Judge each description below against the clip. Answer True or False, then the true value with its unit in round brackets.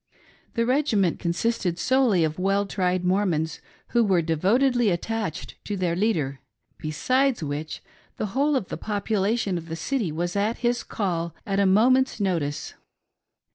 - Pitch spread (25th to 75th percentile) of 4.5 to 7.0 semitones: True (5.4 semitones)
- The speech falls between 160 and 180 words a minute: False (150 wpm)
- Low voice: False (195 Hz)